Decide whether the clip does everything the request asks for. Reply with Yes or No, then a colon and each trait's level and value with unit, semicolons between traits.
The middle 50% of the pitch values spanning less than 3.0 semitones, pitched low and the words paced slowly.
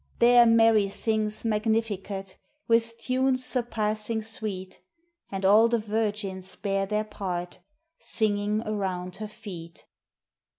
No: narrow, 2.5 semitones; high, 215 Hz; slow, 110 wpm